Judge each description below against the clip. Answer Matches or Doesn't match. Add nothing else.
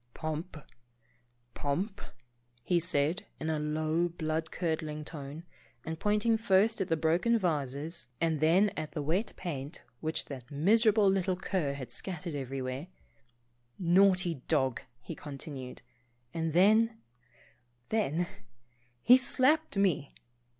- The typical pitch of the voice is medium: Matches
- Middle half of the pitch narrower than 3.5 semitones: Doesn't match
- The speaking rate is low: Matches